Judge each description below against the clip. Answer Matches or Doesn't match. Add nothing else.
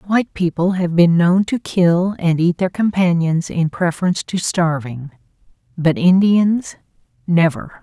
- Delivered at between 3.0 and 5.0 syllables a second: Matches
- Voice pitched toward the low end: Doesn't match